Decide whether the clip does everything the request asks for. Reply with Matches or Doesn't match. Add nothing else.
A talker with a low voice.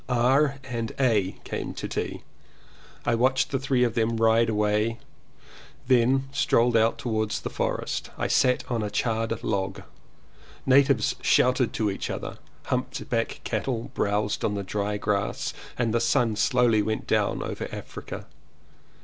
Matches